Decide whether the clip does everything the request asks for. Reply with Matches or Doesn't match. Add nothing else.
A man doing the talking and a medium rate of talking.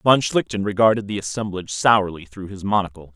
Matches